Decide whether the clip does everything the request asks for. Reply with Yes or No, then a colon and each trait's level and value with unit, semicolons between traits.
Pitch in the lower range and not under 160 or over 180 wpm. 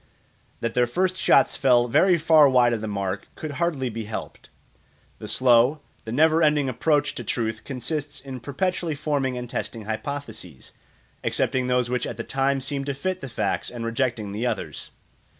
Yes: low, 130 Hz; average, 175 wpm